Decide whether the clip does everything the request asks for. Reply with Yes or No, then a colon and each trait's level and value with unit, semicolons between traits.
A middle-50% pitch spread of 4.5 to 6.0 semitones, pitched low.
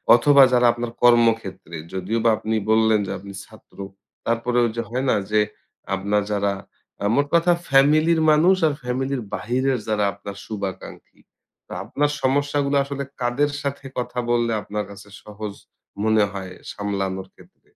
Yes: average, 5.0 semitones; low, 115 Hz